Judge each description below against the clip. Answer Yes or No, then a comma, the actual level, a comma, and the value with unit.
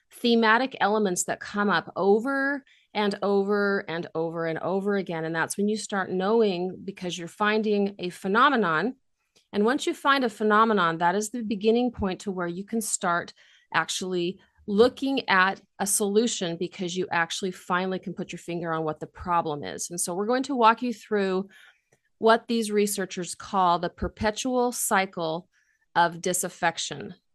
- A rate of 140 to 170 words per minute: Yes, average, 165 wpm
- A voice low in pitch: No, high, 200 Hz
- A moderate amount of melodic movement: Yes, average, 3.9 semitones